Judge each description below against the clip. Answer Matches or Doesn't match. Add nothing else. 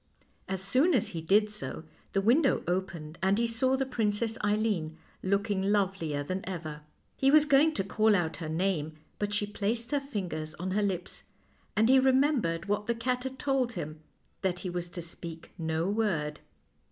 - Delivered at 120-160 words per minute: Doesn't match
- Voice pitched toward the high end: Matches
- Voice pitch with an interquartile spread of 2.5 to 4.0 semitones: Doesn't match